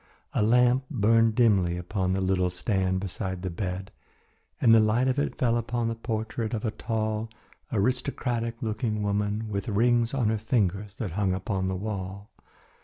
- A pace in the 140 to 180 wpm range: Yes, average, 170 wpm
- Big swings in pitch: No, average, 3.3 semitones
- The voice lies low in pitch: Yes, low, 110 Hz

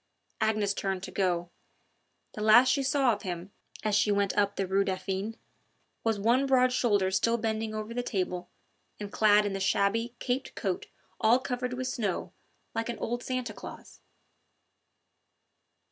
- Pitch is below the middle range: No, high, 215 Hz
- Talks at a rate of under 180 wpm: Yes, average, 160 wpm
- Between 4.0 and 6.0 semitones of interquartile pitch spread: No, average, 3.5 semitones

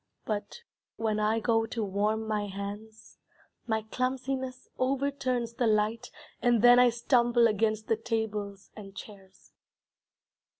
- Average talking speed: No, slow, 125 wpm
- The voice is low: No, high, 225 Hz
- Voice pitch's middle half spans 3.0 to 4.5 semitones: No, narrow, 2.4 semitones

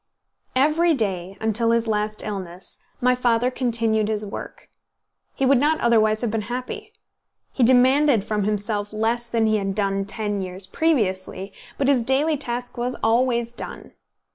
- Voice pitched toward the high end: Yes, high, 230 Hz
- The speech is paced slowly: No, average, 155 wpm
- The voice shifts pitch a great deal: No, average, 3.3 semitones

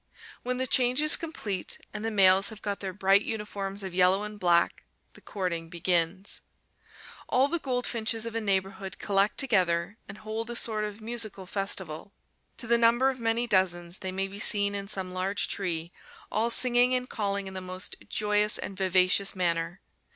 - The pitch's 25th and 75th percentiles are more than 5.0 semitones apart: No, average, 3.3 semitones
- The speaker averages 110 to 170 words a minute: No, average, 180 wpm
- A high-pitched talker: Yes, high, 200 Hz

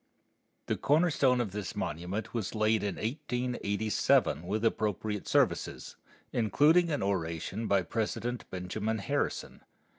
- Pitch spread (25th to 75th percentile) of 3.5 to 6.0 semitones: Yes, average, 3.8 semitones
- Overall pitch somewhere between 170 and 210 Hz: No, low, 110 Hz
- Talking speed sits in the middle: No, slow, 120 wpm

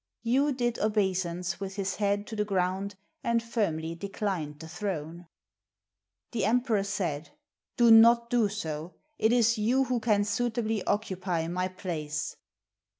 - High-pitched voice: Yes, high, 200 Hz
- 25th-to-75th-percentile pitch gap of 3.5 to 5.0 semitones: Yes, average, 4.2 semitones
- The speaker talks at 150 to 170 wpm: Yes, average, 160 wpm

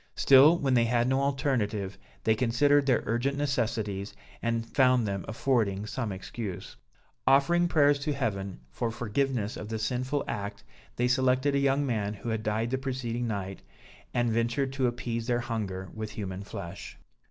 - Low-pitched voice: Yes, low, 120 Hz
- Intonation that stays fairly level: No, average, 4.0 semitones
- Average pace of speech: Yes, average, 165 wpm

